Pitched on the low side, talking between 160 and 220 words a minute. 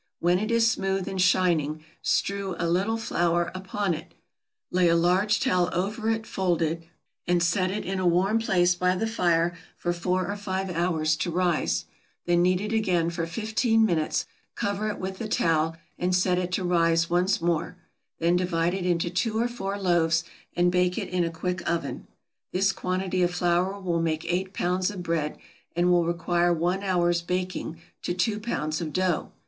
No: medium, 180 Hz; average, 185 wpm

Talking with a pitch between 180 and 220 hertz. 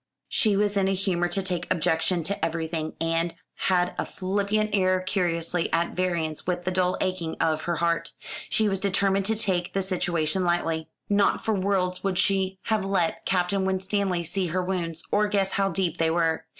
Yes: medium, 185 Hz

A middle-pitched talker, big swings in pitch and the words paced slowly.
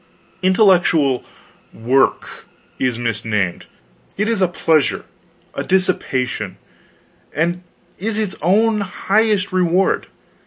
Yes: medium, 180 Hz; wide, 7.4 semitones; slow, 90 wpm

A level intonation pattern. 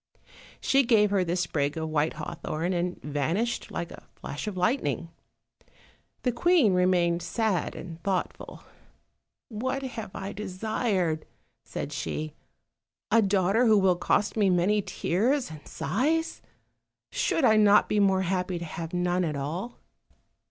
No: average, 4.4 semitones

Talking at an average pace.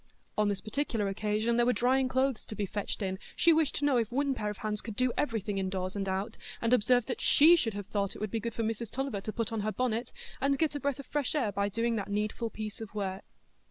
No: fast, 265 wpm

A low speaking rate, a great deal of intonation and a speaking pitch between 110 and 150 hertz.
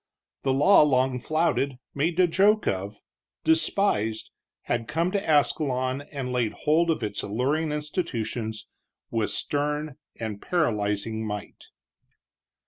Yes: slow, 120 wpm; wide, 6.0 semitones; low, 135 Hz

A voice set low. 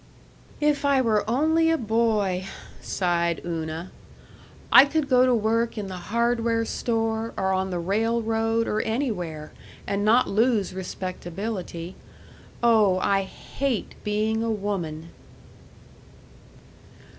No: high, 220 Hz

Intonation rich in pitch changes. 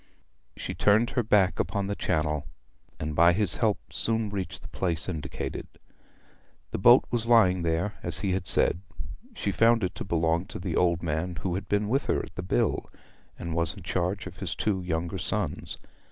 No: average, 3.5 semitones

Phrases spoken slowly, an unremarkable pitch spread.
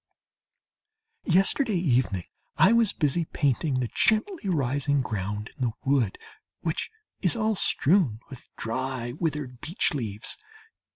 No: slow, 120 wpm; wide, 6.9 semitones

